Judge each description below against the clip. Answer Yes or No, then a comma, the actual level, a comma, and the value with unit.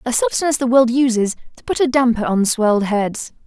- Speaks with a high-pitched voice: Yes, high, 240 Hz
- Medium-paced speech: No, fast, 210 wpm